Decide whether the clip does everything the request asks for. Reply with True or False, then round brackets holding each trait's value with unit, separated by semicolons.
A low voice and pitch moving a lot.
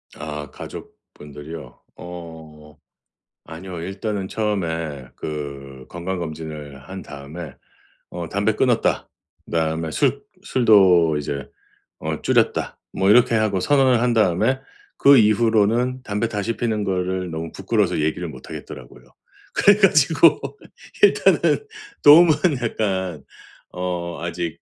True (90 Hz; 5.8 semitones)